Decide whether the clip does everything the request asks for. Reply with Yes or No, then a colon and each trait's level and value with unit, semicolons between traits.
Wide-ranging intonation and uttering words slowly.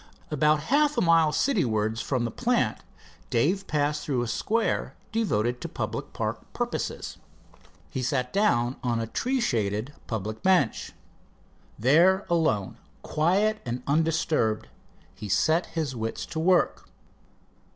Yes: wide, 7.1 semitones; slow, 130 wpm